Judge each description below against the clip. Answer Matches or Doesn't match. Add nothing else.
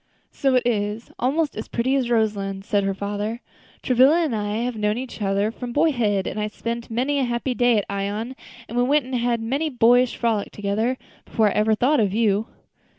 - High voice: Matches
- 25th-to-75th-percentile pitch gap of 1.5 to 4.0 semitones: Matches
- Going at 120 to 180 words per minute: Doesn't match